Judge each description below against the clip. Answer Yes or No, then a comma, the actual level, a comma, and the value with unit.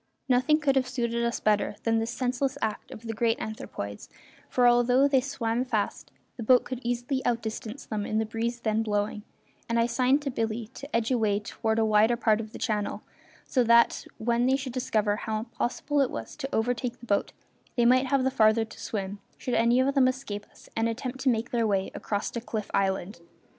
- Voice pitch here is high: Yes, high, 235 Hz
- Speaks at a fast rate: Yes, fast, 210 wpm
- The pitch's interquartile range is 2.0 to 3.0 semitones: Yes, average, 2.7 semitones